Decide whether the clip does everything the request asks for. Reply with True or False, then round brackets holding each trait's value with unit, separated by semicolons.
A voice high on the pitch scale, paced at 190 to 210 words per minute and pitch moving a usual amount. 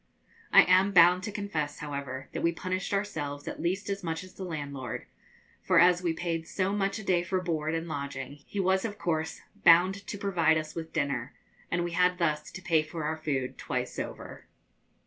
False (170 Hz; 200 wpm; 3.4 semitones)